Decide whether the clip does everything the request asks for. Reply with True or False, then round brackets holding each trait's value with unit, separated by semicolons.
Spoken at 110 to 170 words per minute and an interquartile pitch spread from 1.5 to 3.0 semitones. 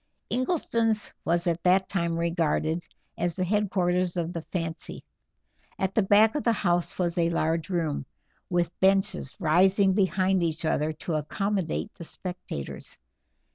True (140 wpm; 2.6 semitones)